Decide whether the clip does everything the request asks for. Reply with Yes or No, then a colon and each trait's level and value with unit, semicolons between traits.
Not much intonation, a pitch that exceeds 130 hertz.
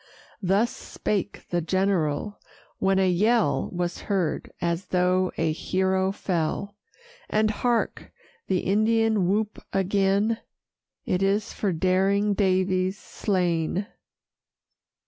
Yes: narrow, 2.1 semitones; high, 190 Hz